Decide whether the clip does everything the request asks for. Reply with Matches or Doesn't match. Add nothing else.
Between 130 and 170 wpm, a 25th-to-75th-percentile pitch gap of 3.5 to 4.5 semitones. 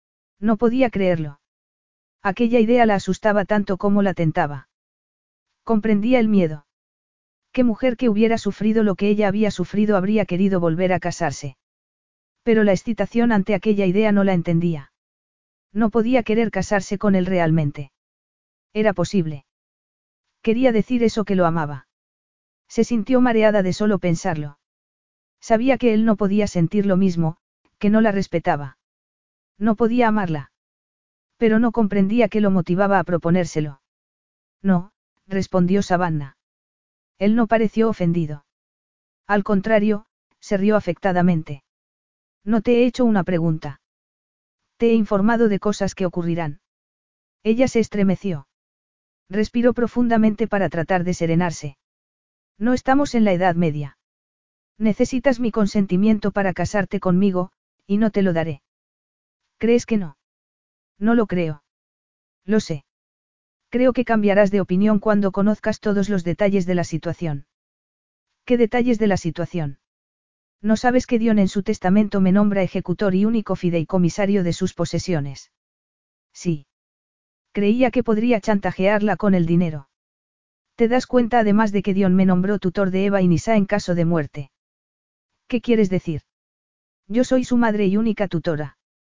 Matches